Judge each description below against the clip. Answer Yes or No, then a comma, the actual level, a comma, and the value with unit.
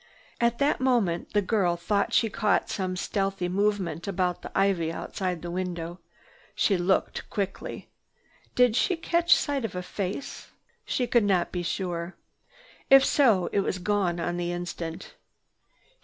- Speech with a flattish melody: No, average, 3.4 semitones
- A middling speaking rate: Yes, average, 150 wpm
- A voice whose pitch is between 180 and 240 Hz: Yes, high, 190 Hz